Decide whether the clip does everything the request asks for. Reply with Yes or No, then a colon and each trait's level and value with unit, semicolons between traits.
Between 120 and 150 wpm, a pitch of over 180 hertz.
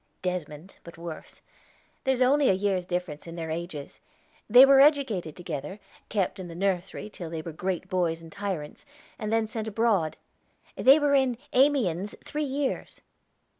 No: average, 160 wpm; high, 190 Hz